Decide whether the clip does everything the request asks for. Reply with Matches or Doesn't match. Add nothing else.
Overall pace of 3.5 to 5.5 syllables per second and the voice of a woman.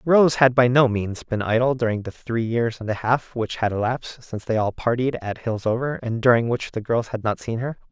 Doesn't match